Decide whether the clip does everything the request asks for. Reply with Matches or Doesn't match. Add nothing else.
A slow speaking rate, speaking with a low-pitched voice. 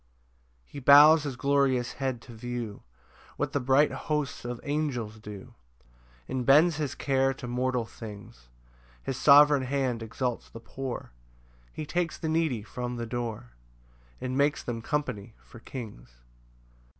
Doesn't match